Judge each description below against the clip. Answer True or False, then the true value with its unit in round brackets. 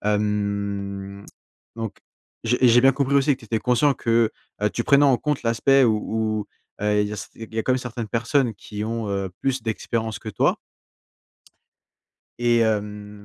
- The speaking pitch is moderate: False (115 Hz)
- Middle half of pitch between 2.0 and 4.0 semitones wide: True (2.9 semitones)